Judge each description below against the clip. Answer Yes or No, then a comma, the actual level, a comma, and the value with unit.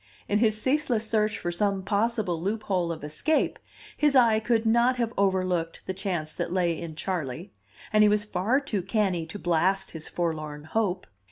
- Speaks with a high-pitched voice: Yes, high, 195 Hz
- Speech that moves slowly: No, average, 175 wpm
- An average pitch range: Yes, average, 4.3 semitones